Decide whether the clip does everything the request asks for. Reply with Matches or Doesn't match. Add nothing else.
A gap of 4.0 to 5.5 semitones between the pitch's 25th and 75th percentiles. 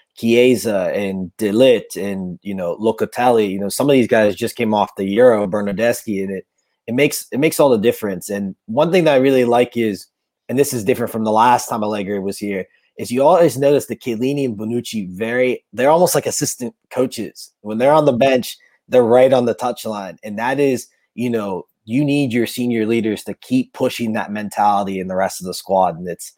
Doesn't match